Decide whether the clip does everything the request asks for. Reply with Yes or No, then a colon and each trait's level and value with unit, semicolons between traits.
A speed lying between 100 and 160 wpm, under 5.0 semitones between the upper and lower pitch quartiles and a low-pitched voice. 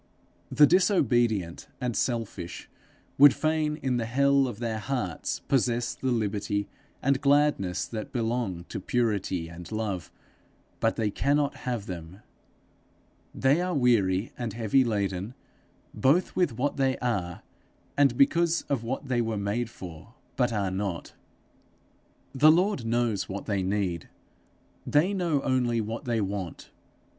No: slow, 135 wpm; average, 5.3 semitones; low, 120 Hz